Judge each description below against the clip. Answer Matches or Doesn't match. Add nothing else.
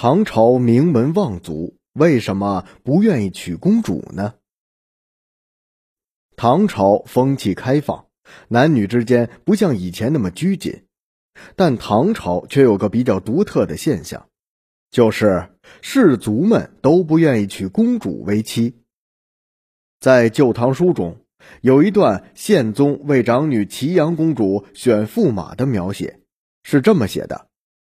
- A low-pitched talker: Matches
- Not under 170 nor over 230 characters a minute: Matches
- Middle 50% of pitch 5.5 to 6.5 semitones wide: Doesn't match